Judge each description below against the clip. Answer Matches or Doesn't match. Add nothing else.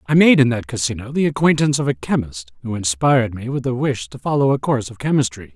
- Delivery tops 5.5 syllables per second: Matches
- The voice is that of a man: Matches